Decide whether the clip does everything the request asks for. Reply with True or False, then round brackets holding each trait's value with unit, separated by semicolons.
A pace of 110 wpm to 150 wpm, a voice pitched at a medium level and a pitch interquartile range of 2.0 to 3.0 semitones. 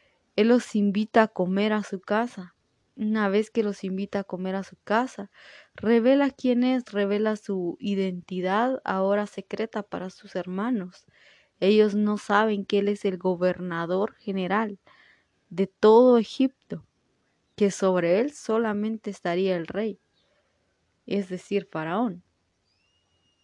False (130 wpm; 205 Hz; 2.6 semitones)